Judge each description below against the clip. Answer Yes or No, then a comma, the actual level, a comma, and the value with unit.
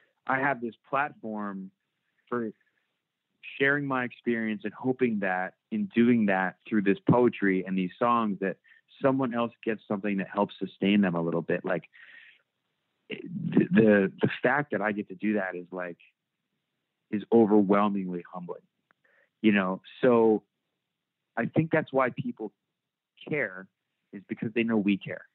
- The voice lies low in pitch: Yes, low, 105 Hz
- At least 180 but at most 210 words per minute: No, average, 150 wpm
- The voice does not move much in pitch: No, average, 3.8 semitones